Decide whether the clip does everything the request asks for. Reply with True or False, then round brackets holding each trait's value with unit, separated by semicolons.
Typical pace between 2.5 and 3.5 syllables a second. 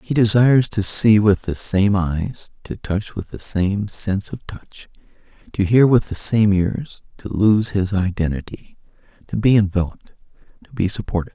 False (4.6 syllables/s)